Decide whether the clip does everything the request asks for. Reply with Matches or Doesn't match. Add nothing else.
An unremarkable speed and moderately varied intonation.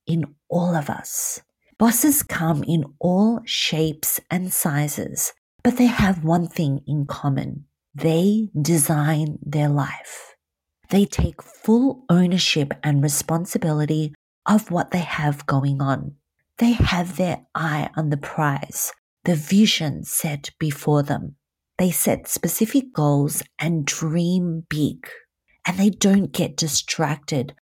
Doesn't match